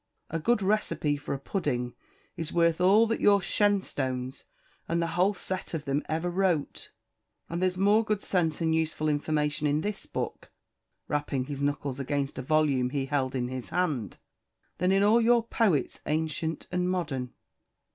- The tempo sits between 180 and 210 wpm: No, average, 165 wpm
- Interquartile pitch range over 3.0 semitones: Yes, average, 4.8 semitones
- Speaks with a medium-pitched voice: Yes, medium, 160 Hz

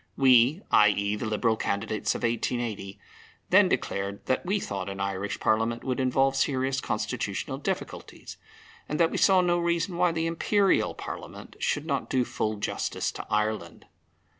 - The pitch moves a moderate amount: No, wide, 7.2 semitones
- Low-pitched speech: Yes, low, 125 Hz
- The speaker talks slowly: No, average, 155 wpm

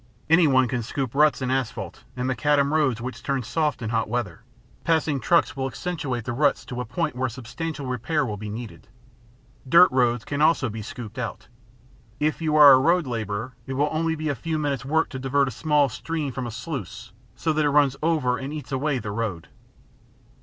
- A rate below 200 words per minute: No, fast, 205 wpm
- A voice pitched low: Yes, low, 130 Hz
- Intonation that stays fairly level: No, average, 4.1 semitones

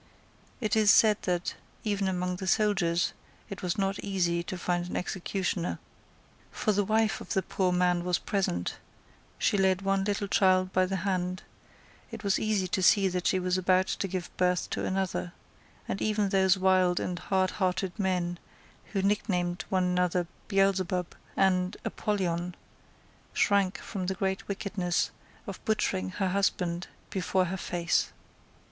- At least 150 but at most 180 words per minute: Yes, average, 155 wpm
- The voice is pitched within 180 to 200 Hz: Yes, medium, 185 Hz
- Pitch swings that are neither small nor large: No, narrow, 1.6 semitones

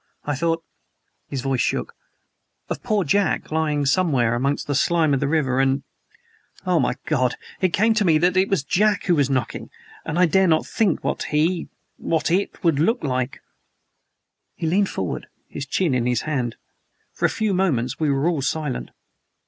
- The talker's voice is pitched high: No, medium, 155 Hz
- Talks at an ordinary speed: Yes, average, 180 wpm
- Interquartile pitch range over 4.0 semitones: Yes, average, 5.0 semitones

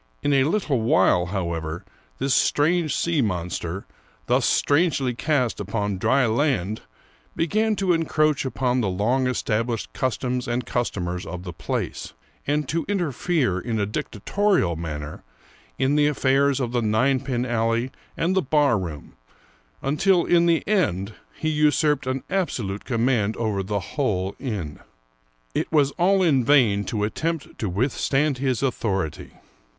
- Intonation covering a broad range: Yes, wide, 6.4 semitones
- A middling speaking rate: Yes, average, 145 wpm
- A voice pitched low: Yes, low, 125 Hz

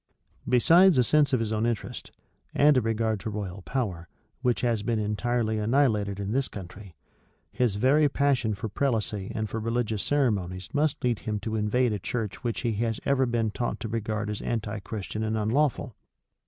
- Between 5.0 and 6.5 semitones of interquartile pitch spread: No, average, 3.1 semitones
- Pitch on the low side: Yes, low, 110 Hz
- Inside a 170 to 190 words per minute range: Yes, average, 180 wpm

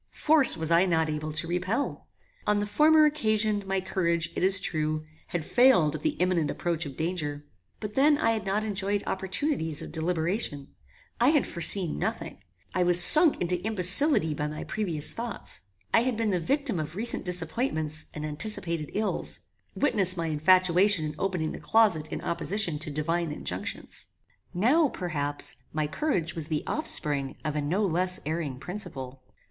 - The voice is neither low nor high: Yes, medium, 180 Hz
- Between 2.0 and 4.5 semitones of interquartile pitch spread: No, average, 5.3 semitones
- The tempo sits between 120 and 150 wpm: No, average, 165 wpm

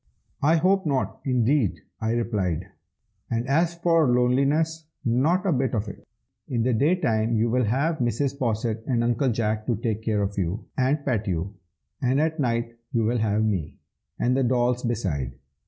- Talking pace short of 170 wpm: No, average, 175 wpm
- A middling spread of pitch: Yes, average, 4.0 semitones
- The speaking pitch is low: Yes, low, 120 Hz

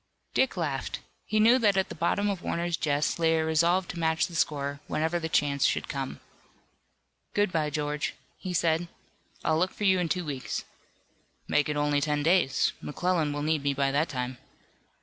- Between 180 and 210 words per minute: Yes, average, 190 wpm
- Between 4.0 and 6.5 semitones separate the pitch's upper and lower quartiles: No, average, 3.2 semitones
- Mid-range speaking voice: Yes, medium, 160 Hz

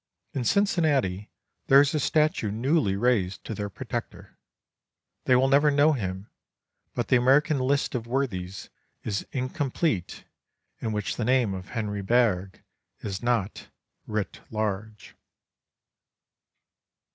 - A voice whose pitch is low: Yes, low, 120 Hz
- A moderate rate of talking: No, slow, 120 wpm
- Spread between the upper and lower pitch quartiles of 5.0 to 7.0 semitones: Yes, average, 5.3 semitones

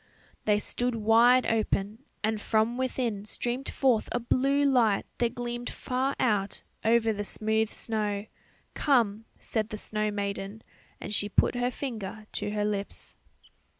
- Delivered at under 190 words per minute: Yes, average, 145 wpm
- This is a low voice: No, high, 220 Hz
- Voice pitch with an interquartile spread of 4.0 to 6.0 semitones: No, average, 2.7 semitones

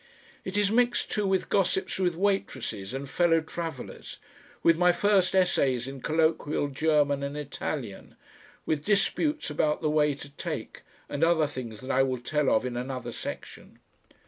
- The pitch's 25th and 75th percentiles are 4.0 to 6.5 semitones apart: Yes, average, 4.8 semitones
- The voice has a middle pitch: Yes, medium, 150 Hz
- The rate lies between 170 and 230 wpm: No, average, 160 wpm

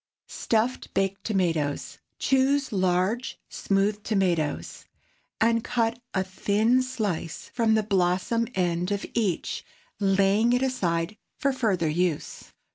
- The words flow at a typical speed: No, slow, 120 wpm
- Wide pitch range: No, average, 4.3 semitones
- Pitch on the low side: No, high, 200 Hz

